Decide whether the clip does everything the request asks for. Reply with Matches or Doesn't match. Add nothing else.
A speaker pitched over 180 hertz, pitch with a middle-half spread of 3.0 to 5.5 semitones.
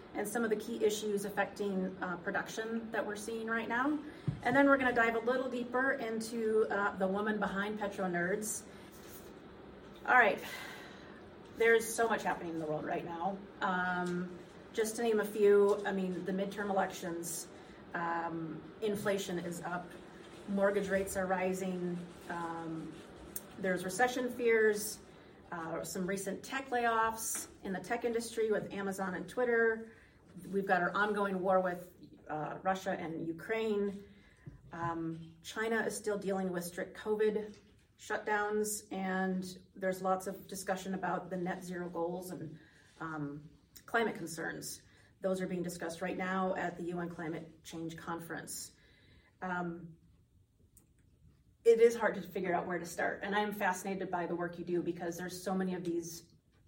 Matches